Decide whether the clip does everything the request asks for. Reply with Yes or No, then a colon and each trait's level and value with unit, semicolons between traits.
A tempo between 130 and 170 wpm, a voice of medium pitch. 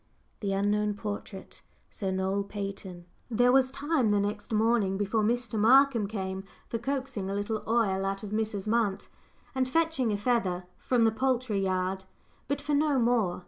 No: average, 165 wpm; high, 215 Hz